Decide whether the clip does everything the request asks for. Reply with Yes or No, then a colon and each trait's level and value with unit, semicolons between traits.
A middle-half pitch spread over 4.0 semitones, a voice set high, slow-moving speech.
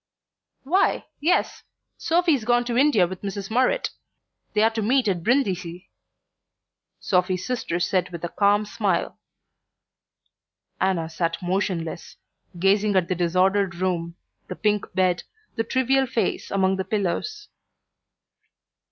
Yes: average, 4.9 semitones; high, 195 Hz; slow, 120 wpm